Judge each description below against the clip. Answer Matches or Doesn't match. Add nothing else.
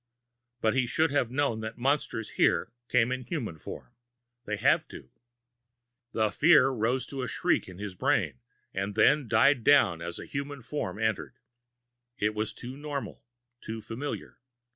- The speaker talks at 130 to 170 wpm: Matches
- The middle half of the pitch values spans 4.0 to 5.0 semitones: Matches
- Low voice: Matches